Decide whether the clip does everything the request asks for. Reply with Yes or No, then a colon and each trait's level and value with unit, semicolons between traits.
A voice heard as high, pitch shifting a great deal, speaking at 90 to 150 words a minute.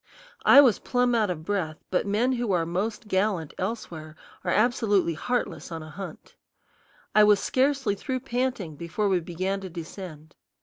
No: high, 200 Hz; wide, 5.8 semitones; average, 165 wpm